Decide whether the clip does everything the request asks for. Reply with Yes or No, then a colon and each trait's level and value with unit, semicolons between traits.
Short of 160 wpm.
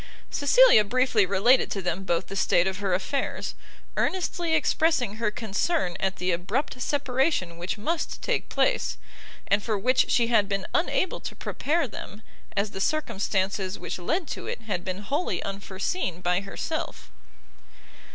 Yes: average, 150 wpm